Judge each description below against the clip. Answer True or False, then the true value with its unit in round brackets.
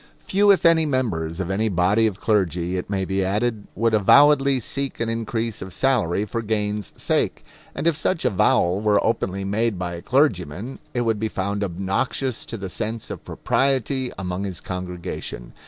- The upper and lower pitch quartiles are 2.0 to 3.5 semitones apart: False (4.7 semitones)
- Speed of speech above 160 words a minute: True (175 wpm)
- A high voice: False (105 Hz)